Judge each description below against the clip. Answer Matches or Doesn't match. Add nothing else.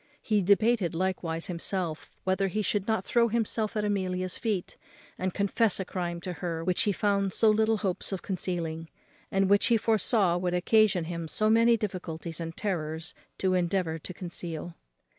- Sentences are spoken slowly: Doesn't match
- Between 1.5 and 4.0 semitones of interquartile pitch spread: Matches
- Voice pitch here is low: Doesn't match